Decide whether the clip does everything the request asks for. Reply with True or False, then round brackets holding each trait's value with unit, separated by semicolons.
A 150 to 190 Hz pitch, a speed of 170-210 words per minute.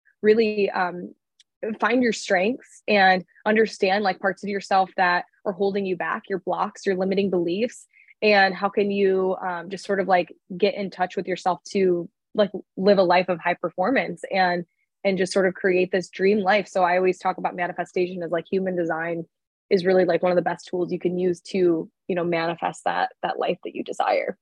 True (185 Hz; 205 wpm)